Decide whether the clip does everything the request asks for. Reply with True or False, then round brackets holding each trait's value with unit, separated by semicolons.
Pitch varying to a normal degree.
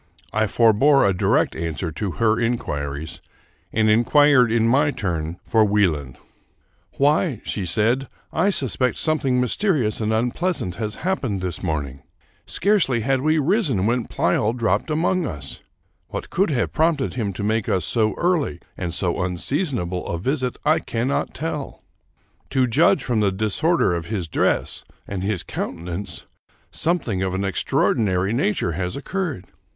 False (7.1 semitones)